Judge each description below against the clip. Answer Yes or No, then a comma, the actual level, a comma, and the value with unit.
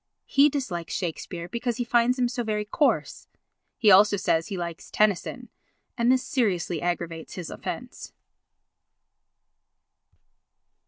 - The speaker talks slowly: Yes, slow, 120 wpm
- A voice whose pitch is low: No, high, 210 Hz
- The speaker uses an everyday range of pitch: No, wide, 5.7 semitones